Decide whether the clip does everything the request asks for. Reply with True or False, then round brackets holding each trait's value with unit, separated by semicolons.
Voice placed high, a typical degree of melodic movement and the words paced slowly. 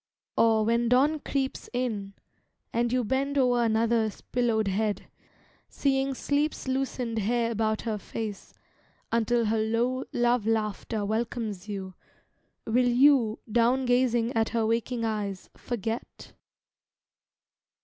False (230 Hz; 2.3 semitones; 120 wpm)